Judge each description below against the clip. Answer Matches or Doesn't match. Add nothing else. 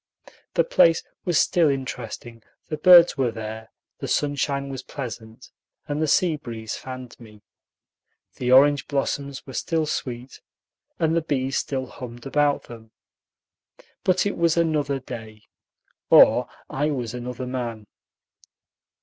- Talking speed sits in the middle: Doesn't match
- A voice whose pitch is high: Doesn't match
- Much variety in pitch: Doesn't match